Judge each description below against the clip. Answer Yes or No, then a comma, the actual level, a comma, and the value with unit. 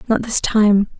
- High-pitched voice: Yes, high, 215 Hz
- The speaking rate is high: No, average, 180 wpm